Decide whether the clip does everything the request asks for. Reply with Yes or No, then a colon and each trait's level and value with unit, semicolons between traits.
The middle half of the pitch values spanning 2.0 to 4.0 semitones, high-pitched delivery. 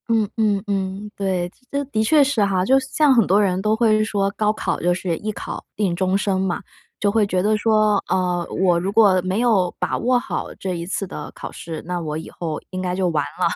Yes: average, 2.9 semitones; high, 195 Hz